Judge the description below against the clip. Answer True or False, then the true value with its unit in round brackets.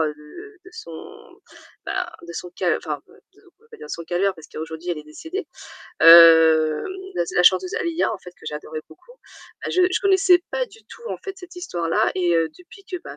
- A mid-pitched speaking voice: True (180 Hz)